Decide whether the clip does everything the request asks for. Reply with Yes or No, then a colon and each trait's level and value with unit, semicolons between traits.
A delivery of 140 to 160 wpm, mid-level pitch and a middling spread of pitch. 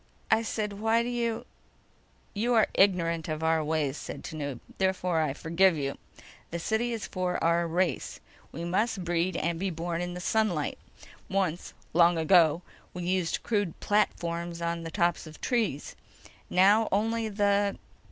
Yes: average, 150 wpm; medium, 180 Hz; average, 3.7 semitones